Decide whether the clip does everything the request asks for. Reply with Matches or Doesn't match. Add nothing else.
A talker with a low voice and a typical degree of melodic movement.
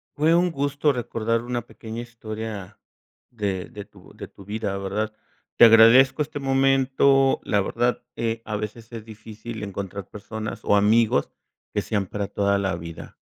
Matches